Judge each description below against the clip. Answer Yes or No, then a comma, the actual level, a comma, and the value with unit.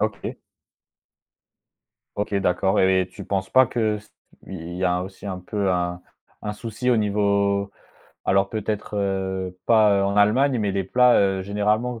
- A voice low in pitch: Yes, low, 100 Hz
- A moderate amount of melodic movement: No, narrow, 2.0 semitones